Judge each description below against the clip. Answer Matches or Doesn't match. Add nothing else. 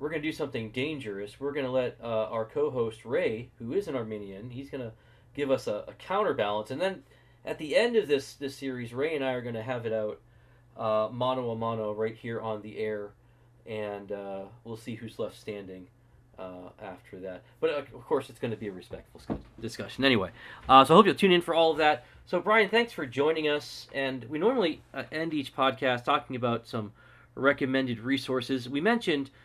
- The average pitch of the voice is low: Matches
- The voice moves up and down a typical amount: Matches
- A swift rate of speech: Matches